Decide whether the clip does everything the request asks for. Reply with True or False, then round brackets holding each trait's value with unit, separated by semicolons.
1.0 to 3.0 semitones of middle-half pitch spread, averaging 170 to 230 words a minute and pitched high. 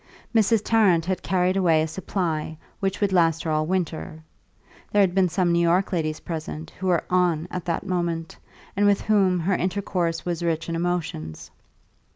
False (2.5 semitones; 180 wpm; 175 Hz)